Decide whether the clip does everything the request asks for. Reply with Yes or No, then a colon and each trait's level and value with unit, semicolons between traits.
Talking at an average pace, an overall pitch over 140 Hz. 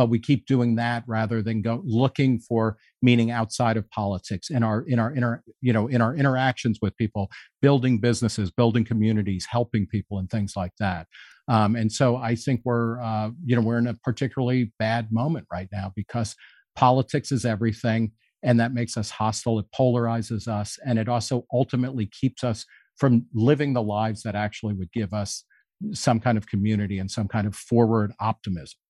No: average, 190 wpm; low, 115 Hz